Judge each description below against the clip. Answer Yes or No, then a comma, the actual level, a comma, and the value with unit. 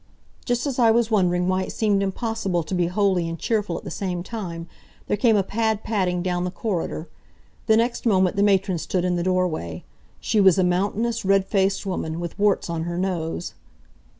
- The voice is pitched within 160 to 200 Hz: Yes, high, 190 Hz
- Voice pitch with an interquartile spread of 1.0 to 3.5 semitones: Yes, average, 3.1 semitones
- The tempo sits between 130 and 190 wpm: No, average, 200 wpm